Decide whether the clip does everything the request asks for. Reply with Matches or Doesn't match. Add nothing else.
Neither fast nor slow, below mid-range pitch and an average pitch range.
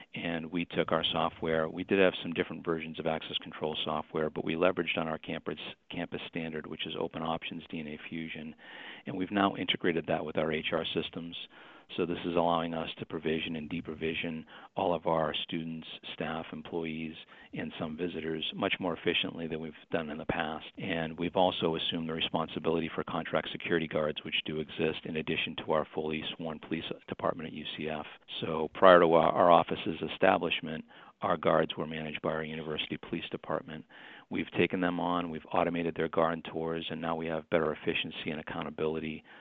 Doesn't match